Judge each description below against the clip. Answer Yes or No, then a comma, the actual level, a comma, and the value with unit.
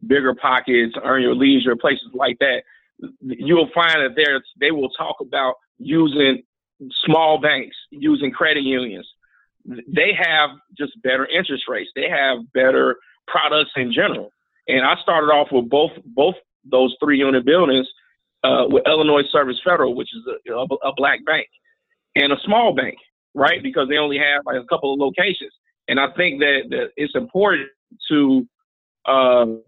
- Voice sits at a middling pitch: Yes, medium, 150 Hz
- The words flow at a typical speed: Yes, average, 160 wpm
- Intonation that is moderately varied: No, wide, 6.6 semitones